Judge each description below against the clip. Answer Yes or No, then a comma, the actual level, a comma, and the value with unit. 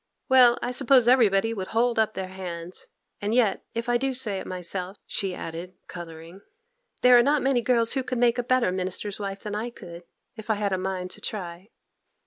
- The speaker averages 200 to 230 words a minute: Yes, fast, 205 wpm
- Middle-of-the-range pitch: No, high, 210 Hz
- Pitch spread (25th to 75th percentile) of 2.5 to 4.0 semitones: No, average, 4.6 semitones